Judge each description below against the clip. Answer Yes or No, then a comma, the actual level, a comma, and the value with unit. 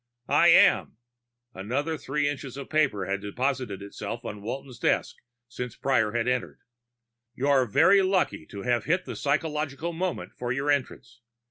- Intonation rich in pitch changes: No, average, 3.9 semitones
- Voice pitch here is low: Yes, low, 130 Hz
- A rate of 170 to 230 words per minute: No, average, 150 wpm